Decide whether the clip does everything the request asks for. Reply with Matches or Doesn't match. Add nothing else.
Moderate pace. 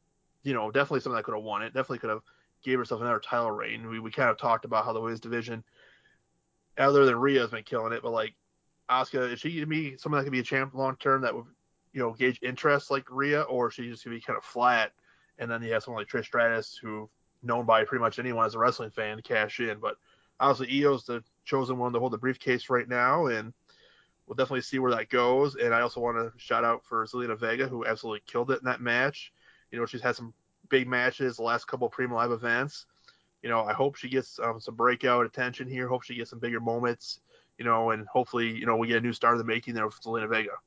Doesn't match